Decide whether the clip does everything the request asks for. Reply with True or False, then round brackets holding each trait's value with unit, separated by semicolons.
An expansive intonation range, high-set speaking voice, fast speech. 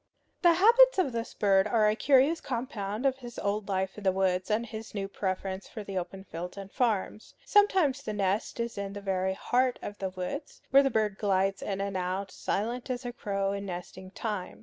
False (4.2 semitones; 205 Hz; 210 wpm)